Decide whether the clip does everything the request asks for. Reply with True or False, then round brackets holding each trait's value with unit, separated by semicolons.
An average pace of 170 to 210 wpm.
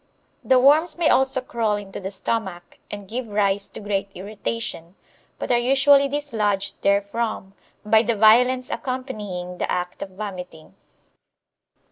False (135 wpm)